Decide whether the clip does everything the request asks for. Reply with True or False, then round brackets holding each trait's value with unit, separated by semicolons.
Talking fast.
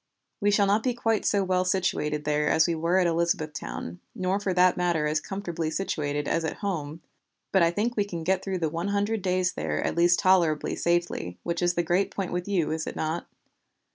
True (215 wpm)